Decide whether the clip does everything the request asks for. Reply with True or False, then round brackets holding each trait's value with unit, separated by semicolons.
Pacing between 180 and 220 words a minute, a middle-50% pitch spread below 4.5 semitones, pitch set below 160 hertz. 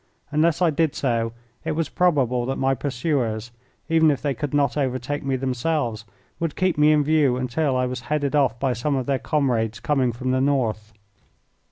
True (190 wpm; 3.4 semitones; 135 Hz)